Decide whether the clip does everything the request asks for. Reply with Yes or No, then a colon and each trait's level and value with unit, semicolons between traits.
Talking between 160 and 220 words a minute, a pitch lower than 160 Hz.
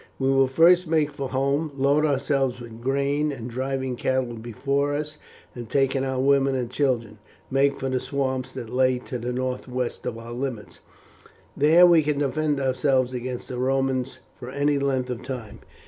Yes: average, 175 wpm; low, 135 Hz